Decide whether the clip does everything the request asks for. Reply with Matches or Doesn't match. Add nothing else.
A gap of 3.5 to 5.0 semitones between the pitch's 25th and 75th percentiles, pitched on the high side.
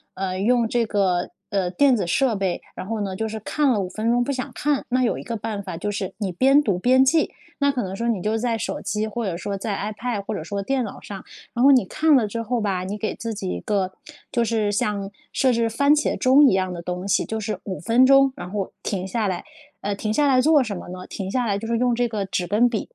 Matches